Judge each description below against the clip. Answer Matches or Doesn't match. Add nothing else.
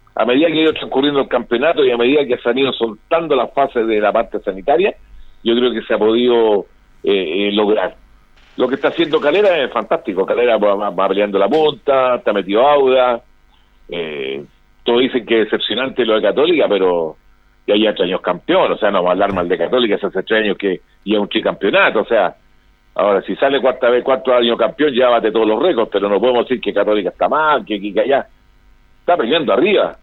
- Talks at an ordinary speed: Doesn't match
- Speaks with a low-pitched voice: Matches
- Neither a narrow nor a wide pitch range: Matches